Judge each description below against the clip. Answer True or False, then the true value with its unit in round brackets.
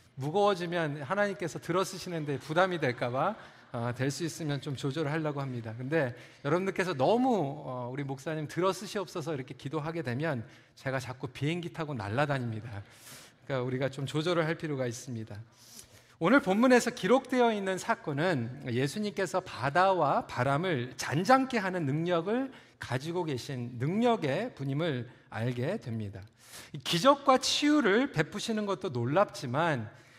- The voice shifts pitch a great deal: True (6.7 semitones)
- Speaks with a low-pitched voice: False (150 Hz)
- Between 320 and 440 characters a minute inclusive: True (340 characters per minute)